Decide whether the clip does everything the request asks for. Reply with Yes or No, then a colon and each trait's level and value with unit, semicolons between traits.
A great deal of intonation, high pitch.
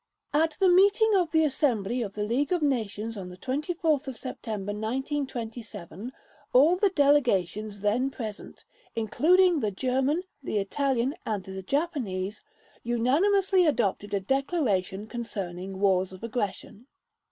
Yes: wide, 6.3 semitones; high, 240 Hz